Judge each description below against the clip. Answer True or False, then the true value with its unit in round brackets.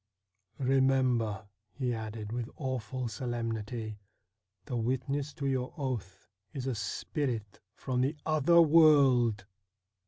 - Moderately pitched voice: False (125 Hz)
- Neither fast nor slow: False (120 wpm)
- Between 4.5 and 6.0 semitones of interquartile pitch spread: False (3.5 semitones)